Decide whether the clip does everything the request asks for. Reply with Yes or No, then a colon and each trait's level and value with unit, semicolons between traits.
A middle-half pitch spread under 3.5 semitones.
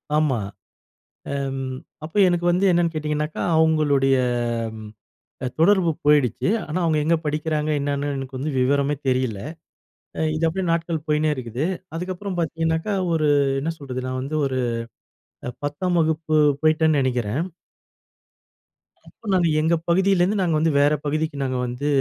Yes: average, 3.1 semitones